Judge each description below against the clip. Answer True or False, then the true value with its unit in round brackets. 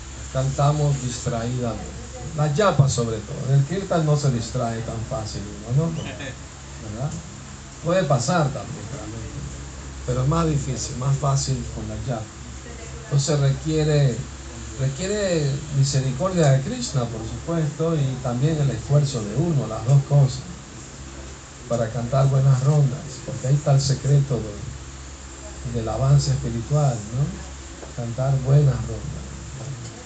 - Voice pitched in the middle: False (130 Hz)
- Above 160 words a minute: False (125 wpm)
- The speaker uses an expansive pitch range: False (4.4 semitones)